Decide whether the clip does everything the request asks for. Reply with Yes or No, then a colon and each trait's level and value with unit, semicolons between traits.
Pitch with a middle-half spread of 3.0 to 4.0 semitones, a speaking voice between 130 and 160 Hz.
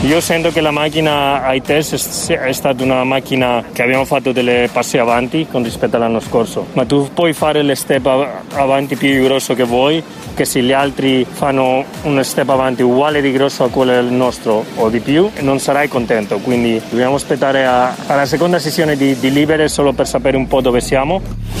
No: narrow, 2.4 semitones; low, 135 Hz